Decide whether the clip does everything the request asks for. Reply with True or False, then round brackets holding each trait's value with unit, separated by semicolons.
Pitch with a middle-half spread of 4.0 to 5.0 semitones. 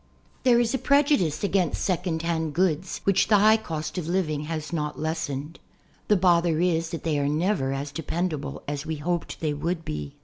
False (3.3 semitones)